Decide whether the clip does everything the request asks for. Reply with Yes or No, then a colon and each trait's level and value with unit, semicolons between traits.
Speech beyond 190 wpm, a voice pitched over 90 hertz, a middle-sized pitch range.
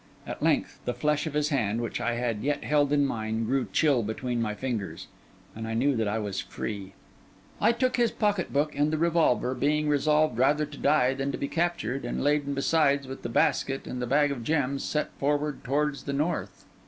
Yes: fast, 205 wpm; medium, 140 Hz; average, 3.5 semitones